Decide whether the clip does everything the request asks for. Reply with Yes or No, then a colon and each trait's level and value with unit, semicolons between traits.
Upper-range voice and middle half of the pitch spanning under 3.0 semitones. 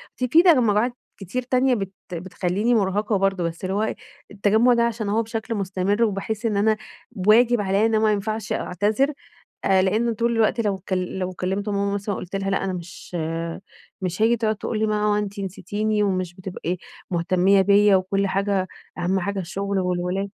Yes: high, 200 Hz; narrow, 2.5 semitones